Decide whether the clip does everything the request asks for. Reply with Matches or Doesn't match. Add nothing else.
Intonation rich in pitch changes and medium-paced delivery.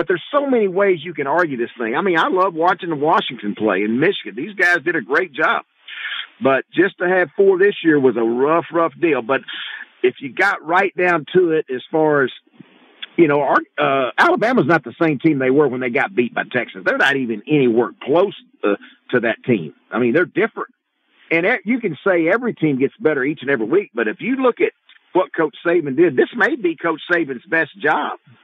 Doesn't match